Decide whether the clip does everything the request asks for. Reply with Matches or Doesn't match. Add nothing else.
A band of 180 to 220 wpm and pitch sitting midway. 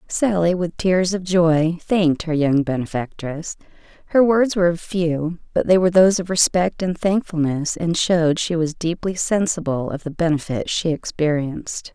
Doesn't match